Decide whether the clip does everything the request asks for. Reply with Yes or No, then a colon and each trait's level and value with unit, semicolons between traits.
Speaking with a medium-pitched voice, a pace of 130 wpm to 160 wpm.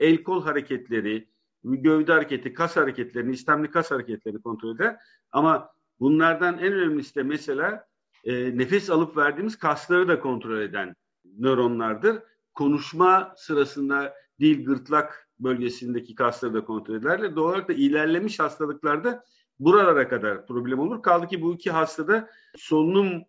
Yes: medium, 150 Hz; average, 135 wpm